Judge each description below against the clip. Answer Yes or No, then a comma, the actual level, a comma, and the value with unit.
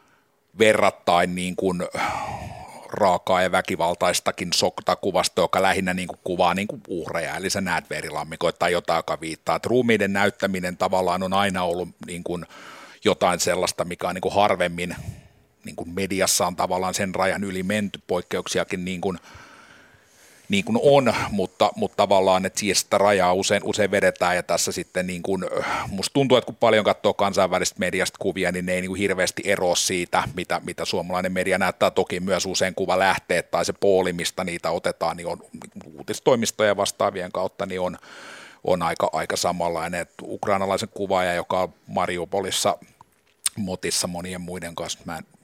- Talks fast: Yes, fast, 165 wpm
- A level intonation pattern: Yes, narrow, 1.5 semitones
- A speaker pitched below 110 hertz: Yes, very low, 90 Hz